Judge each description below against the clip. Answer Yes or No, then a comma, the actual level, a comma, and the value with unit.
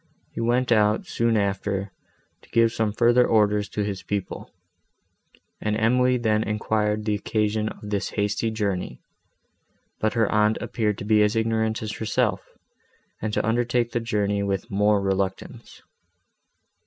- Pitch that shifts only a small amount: Yes, narrow, 1.7 semitones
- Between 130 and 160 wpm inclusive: Yes, average, 145 wpm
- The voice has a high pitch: No, low, 105 Hz